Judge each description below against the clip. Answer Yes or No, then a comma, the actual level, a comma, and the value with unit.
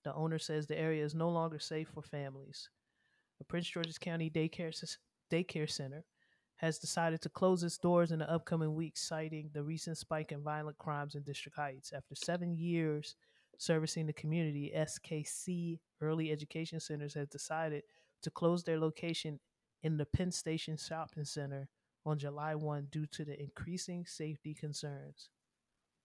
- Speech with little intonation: Yes, narrow, 1.8 semitones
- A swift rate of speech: No, average, 160 wpm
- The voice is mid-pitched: Yes, medium, 155 Hz